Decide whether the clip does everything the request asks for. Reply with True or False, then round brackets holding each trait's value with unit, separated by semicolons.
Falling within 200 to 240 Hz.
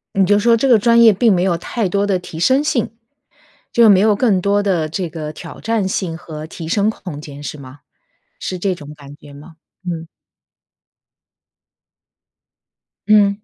False (190 Hz)